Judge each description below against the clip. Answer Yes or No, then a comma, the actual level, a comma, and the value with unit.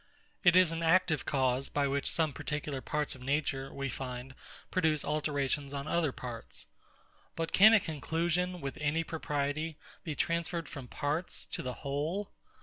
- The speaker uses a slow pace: No, average, 155 wpm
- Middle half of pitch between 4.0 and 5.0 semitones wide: No, average, 3.1 semitones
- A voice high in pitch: No, medium, 150 Hz